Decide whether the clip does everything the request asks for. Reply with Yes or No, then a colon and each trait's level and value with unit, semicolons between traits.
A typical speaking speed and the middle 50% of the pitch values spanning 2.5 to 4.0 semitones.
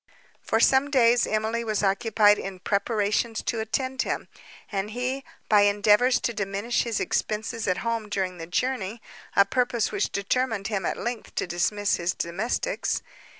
Yes: average, 150 wpm; average, 2.9 semitones